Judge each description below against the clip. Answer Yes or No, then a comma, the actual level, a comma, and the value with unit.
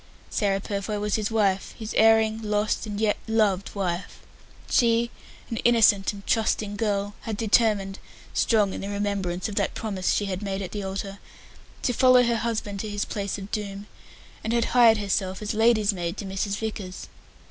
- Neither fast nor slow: Yes, average, 180 wpm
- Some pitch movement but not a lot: No, narrow, 2.0 semitones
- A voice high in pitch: Yes, high, 205 Hz